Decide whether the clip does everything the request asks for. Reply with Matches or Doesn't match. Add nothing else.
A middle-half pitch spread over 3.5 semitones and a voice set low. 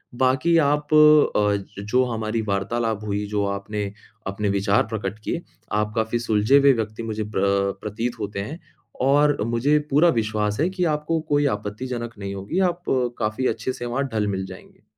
Matches